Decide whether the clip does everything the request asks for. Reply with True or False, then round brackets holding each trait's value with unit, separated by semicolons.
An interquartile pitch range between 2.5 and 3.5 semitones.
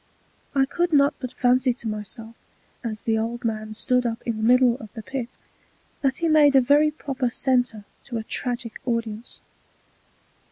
True (3.1 semitones)